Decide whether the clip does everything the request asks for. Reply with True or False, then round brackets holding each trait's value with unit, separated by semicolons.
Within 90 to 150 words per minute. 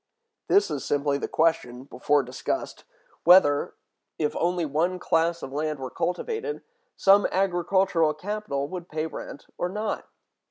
True (135 wpm)